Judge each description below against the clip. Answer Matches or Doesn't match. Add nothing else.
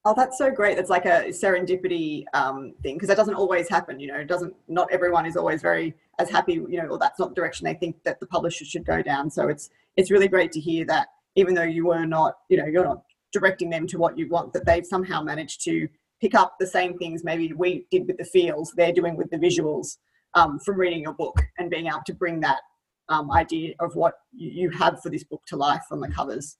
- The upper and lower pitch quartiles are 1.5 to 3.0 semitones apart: Matches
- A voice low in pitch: Doesn't match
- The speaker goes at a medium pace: Doesn't match